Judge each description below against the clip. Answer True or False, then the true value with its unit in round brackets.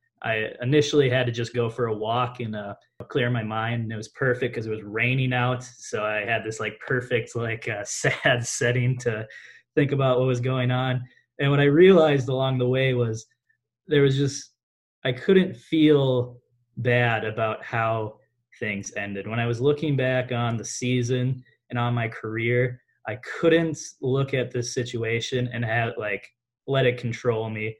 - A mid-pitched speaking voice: False (120 Hz)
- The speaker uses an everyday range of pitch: False (2.3 semitones)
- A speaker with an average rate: True (180 wpm)